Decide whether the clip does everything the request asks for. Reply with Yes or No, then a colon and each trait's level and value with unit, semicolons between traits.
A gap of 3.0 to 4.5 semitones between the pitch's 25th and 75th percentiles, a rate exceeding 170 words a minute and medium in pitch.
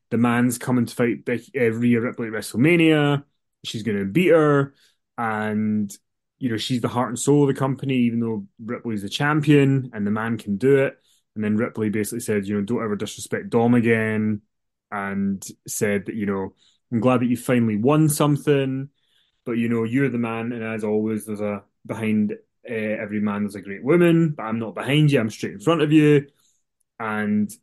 No: average, 4.1 semitones; average, 200 wpm; low, 115 Hz